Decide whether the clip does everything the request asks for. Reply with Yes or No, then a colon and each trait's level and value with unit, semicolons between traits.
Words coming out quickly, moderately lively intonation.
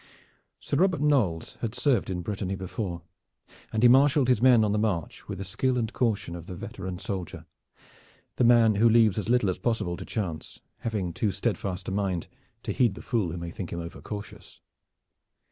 No: average, 190 wpm; average, 4.3 semitones